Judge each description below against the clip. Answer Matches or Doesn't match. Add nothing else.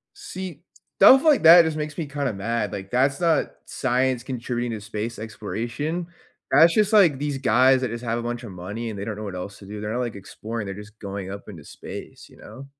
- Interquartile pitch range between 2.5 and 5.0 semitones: Doesn't match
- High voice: Doesn't match